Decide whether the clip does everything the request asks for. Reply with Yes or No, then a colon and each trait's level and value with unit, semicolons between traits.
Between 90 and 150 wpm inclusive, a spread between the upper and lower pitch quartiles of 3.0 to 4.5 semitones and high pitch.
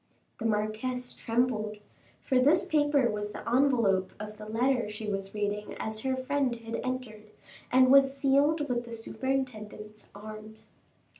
Yes: average, 145 wpm; average, 3.7 semitones; high, 235 Hz